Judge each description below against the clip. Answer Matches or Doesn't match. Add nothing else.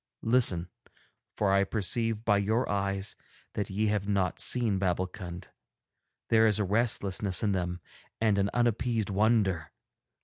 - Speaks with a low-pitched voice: Matches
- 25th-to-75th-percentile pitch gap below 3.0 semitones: Matches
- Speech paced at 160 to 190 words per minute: Doesn't match